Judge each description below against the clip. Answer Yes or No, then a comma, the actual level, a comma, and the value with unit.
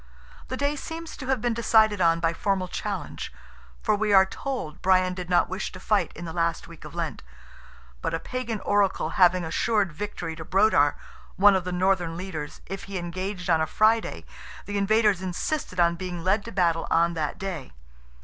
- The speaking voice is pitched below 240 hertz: Yes, medium, 185 Hz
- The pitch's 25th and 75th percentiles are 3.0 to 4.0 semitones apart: Yes, average, 3.7 semitones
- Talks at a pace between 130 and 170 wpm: No, average, 190 wpm